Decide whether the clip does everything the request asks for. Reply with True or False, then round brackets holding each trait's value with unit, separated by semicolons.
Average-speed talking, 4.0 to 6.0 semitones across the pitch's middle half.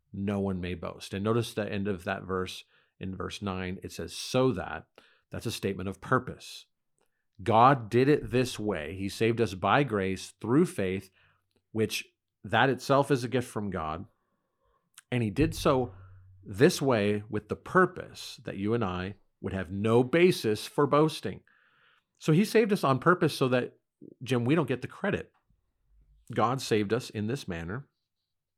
True (170 wpm; 5.2 semitones)